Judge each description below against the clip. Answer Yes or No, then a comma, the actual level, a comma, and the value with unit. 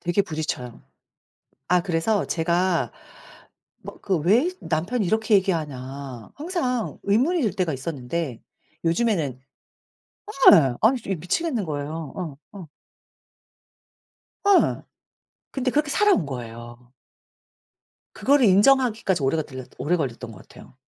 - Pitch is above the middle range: No, medium, 175 Hz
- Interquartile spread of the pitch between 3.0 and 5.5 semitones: No, wide, 7.7 semitones